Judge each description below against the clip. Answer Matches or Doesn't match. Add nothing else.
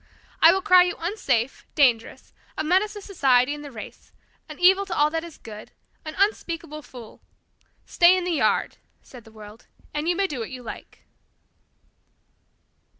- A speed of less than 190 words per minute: Matches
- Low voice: Doesn't match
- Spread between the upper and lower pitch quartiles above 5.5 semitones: Matches